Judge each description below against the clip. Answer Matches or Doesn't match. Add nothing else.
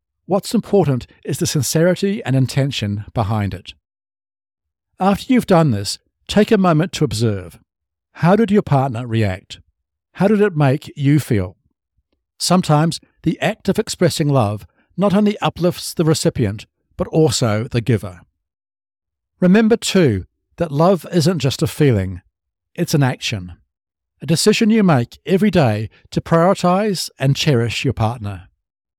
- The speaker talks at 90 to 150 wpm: Matches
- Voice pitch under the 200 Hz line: Matches